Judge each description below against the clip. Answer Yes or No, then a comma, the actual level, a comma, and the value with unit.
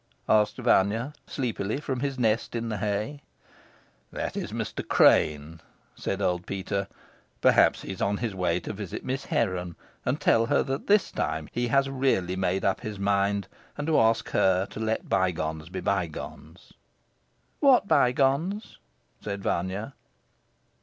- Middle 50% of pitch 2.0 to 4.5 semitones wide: No, average, 5.1 semitones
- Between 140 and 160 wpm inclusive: Yes, average, 150 wpm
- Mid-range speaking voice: No, low, 105 Hz